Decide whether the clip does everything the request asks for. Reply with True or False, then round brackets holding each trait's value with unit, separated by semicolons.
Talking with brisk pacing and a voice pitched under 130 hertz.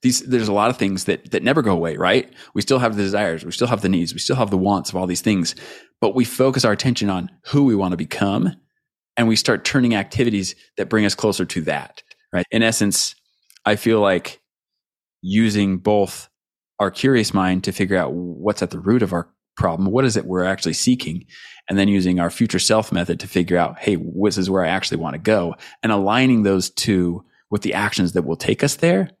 True (230 wpm; 100 Hz)